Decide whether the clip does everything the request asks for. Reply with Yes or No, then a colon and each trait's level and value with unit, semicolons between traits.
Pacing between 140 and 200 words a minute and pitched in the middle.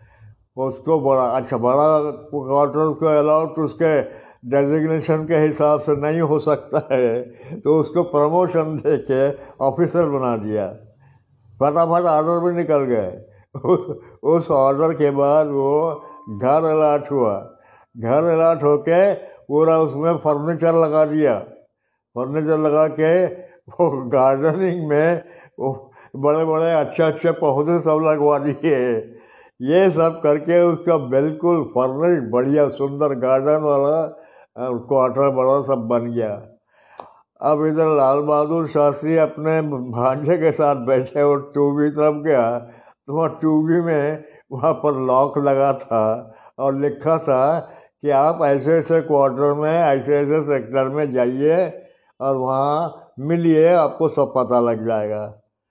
No: average, 130 wpm; medium, 150 Hz